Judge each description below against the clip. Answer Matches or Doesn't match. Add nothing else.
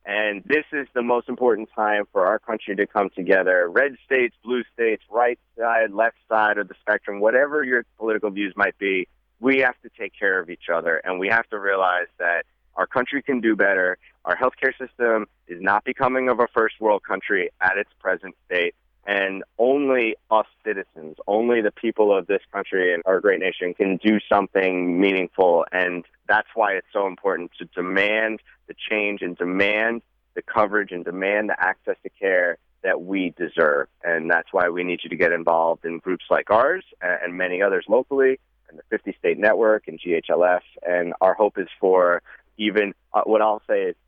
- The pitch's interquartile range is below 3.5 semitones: Doesn't match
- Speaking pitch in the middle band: Doesn't match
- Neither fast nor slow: Matches